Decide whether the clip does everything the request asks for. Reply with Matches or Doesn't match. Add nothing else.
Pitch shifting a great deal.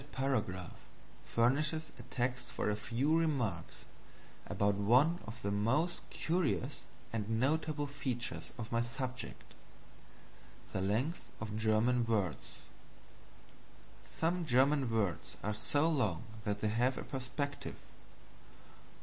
Doesn't match